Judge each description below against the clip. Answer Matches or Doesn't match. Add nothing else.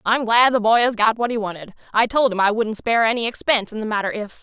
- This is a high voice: Matches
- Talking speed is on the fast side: Matches